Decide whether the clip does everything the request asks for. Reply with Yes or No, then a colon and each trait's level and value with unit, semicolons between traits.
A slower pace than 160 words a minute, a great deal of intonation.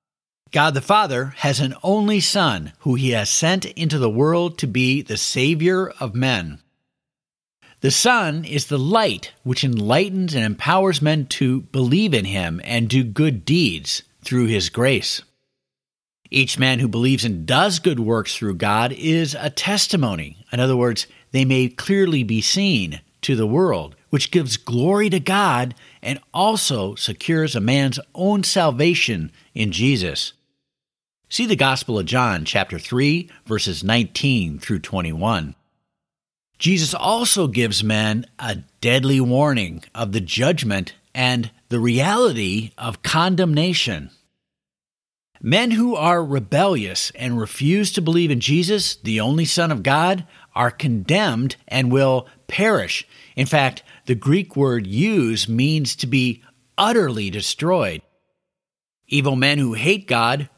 Yes: average, 140 wpm; wide, 6.0 semitones